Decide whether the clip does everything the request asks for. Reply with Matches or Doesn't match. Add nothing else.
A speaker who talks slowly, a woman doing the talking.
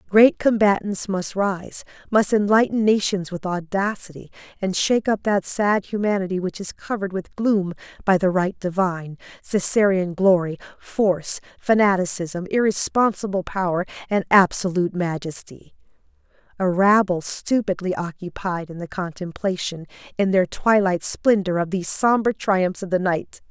Matches